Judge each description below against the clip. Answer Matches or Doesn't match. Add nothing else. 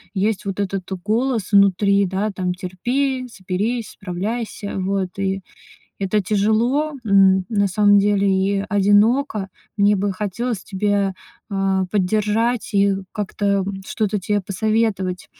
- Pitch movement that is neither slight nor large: Doesn't match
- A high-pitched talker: Matches